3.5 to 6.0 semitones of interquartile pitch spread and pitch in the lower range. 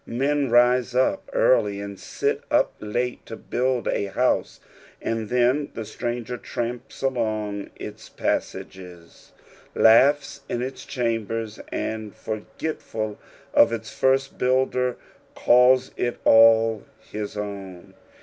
No: average, 2.8 semitones; low, 115 Hz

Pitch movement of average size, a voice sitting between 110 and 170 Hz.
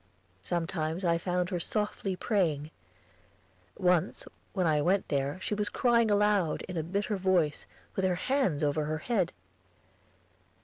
No: average, 4.2 semitones; medium, 180 Hz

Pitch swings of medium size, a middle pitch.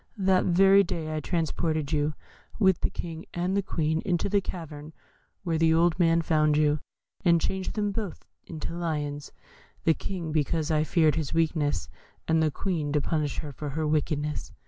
No: narrow, 2.3 semitones; medium, 160 Hz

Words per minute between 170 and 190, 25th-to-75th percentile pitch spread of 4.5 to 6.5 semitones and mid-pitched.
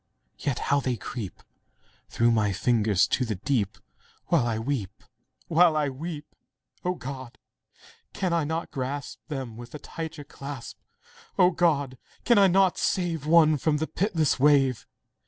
No: average, 145 wpm; average, 4.9 semitones; medium, 145 Hz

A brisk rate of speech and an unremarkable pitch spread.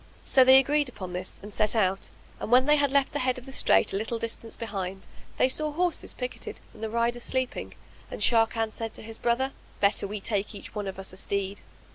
Yes: fast, 225 wpm; average, 4.2 semitones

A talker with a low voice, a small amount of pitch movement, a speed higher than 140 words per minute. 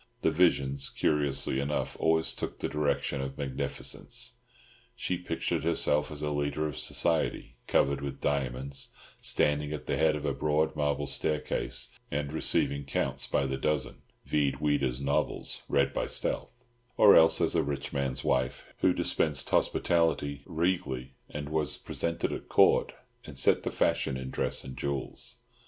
Yes: very low, 70 Hz; narrow, 2.0 semitones; average, 155 wpm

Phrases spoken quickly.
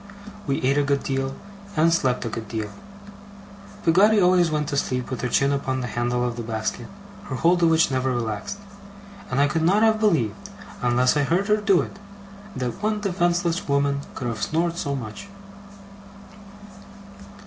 No: average, 180 wpm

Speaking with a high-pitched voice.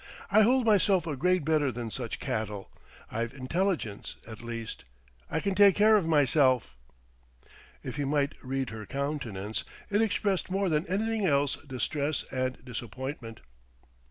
No: medium, 140 Hz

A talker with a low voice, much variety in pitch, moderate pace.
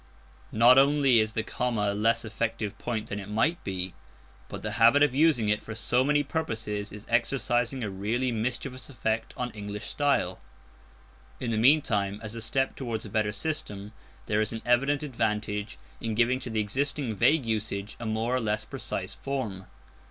No: low, 115 Hz; average, 3.4 semitones; average, 180 wpm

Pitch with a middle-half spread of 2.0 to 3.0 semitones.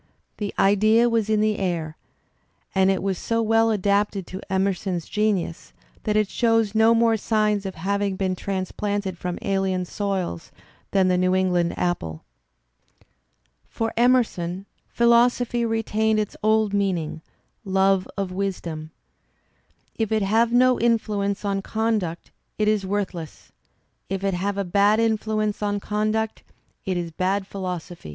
Yes: average, 2.7 semitones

